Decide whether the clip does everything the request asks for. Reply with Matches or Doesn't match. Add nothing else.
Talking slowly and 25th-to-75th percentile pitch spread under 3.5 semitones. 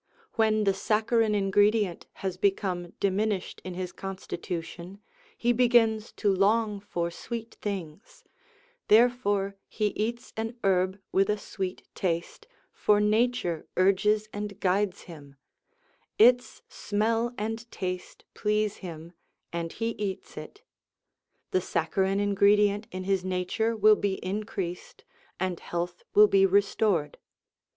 Matches